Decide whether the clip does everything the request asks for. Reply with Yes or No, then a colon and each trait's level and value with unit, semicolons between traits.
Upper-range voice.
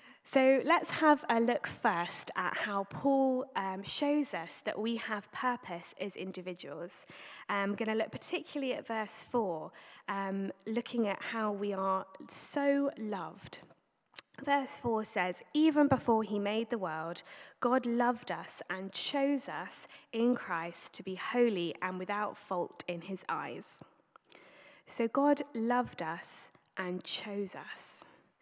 Yes: high, 220 Hz